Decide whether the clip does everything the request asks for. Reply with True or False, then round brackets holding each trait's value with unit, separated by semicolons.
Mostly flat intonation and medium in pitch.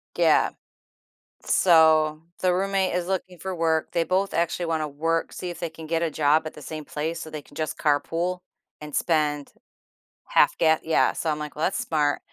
True (2.1 semitones; 160 Hz)